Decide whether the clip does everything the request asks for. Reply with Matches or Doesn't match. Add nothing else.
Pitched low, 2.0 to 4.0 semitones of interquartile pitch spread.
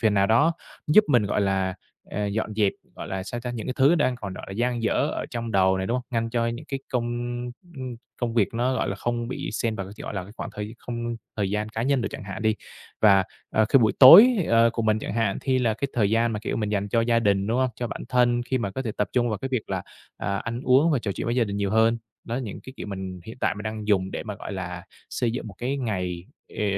Matches